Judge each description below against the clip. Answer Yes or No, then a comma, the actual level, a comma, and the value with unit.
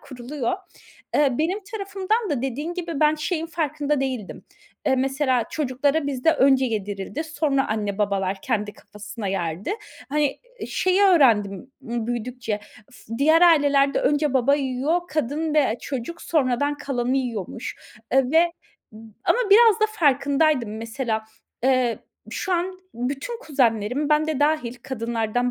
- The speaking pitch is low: No, very high, 270 Hz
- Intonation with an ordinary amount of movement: Yes, average, 4.6 semitones